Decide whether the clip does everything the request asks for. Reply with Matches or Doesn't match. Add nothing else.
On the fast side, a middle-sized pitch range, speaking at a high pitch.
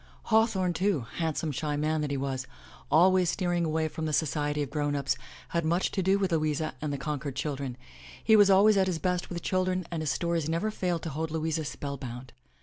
Doesn't match